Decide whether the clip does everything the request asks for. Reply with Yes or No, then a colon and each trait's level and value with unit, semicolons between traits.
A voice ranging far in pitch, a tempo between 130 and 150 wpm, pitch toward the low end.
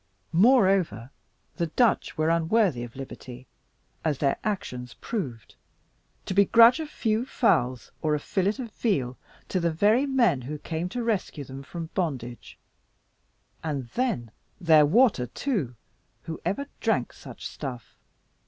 No: wide, 8.9 semitones; slow, 135 wpm; medium, 165 Hz